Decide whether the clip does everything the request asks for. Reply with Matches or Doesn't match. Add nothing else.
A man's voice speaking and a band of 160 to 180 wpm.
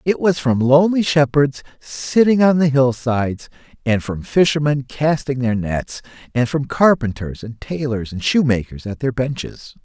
Doesn't match